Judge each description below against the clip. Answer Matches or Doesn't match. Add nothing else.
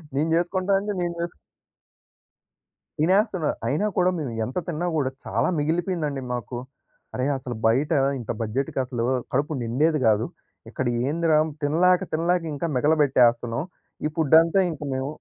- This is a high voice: Doesn't match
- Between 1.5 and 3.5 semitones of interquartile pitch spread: Doesn't match